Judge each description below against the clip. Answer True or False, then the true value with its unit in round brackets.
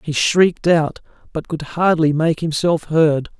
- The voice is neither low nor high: True (160 Hz)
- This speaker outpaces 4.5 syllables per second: False (4.1 syllables/s)